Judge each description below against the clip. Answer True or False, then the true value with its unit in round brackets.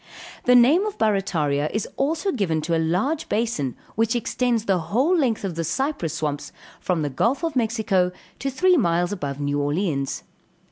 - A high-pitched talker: True (200 Hz)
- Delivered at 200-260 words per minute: False (175 wpm)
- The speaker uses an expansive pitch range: True (7.7 semitones)